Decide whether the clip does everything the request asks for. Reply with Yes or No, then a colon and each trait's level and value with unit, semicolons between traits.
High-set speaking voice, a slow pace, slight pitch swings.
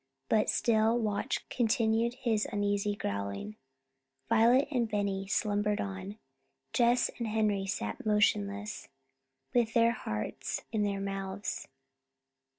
Yes: high, 210 Hz; slow, 110 wpm; narrow, 2.3 semitones